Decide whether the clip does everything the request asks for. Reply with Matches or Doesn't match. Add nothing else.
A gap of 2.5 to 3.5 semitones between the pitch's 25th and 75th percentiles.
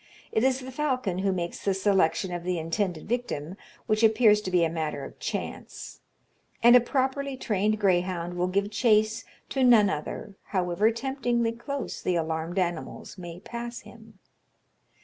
Doesn't match